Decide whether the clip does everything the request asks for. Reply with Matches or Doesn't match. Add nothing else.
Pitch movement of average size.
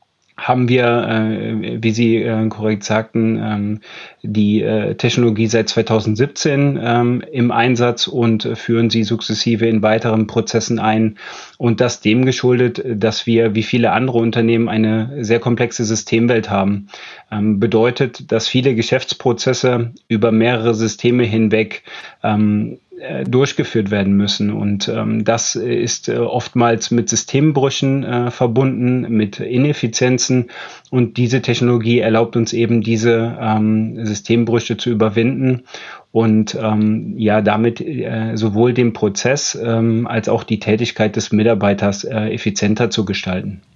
Doesn't match